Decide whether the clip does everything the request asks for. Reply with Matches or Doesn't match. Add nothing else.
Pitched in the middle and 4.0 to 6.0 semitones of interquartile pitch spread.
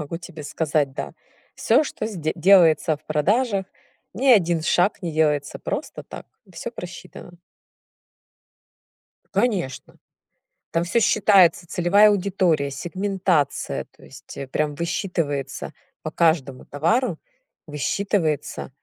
Matches